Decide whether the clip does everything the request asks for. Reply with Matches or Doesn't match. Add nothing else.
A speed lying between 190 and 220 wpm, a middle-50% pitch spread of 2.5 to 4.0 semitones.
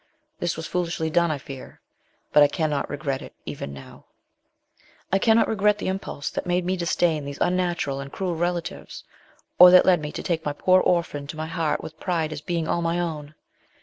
Matches